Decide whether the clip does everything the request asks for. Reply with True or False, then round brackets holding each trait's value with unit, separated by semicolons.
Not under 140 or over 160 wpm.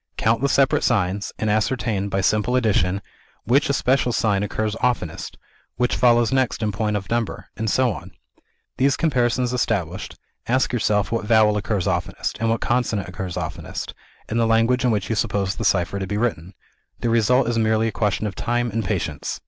False (185 wpm)